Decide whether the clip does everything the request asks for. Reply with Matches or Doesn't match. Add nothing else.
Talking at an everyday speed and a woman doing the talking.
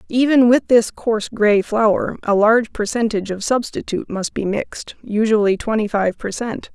Matches